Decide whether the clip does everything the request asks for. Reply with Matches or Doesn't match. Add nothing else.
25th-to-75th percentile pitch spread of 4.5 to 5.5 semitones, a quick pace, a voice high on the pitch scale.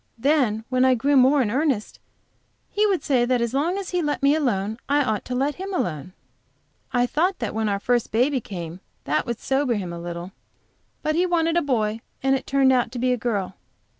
Matches